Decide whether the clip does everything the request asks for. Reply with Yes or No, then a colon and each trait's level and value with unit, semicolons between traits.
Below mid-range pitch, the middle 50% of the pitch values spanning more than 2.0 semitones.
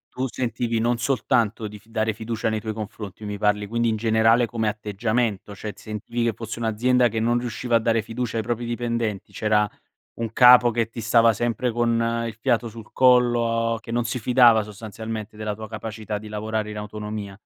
No: low, 115 Hz; narrow, 1.7 semitones